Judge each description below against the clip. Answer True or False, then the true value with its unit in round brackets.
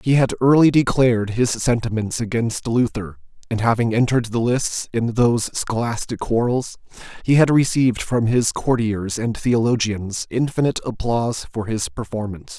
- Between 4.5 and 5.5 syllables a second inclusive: True (5.0 syllables/s)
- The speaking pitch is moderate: False (120 Hz)